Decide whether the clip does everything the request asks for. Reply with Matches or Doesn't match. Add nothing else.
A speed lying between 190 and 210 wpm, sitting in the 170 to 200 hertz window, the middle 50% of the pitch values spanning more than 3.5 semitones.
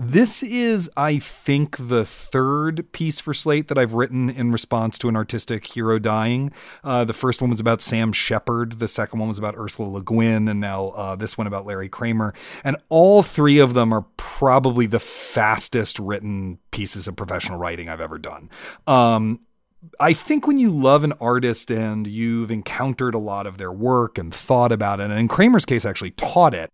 Doesn't match